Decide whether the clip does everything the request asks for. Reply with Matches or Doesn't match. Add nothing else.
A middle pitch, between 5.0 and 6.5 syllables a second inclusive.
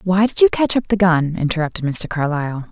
Matches